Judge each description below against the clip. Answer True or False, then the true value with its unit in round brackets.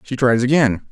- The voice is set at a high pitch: False (125 Hz)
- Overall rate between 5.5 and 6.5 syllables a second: False (5.1 syllables/s)